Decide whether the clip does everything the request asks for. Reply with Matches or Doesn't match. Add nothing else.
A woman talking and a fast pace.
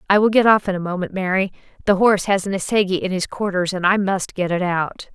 Matches